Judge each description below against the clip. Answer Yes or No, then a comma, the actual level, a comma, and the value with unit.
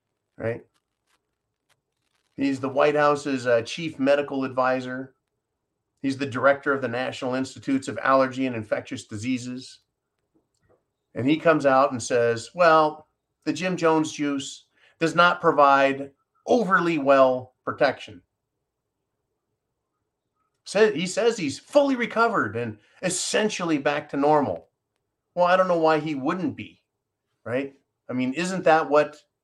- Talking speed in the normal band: No, slow, 130 wpm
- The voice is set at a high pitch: No, medium, 140 Hz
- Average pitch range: Yes, average, 3.7 semitones